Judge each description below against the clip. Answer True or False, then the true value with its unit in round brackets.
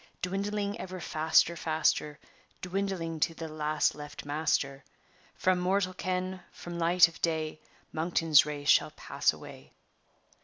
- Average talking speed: False (125 wpm)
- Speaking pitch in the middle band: True (165 Hz)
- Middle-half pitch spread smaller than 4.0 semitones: True (3.0 semitones)